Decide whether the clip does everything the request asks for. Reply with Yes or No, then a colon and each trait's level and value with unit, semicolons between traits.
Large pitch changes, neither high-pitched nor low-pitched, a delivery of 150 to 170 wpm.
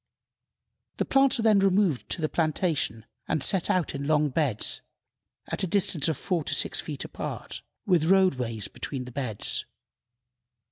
Yes: wide, 5.7 semitones; medium, 160 Hz; average, 155 wpm